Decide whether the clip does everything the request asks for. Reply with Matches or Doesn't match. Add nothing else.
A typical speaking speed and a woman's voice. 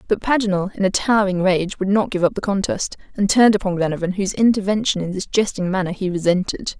Doesn't match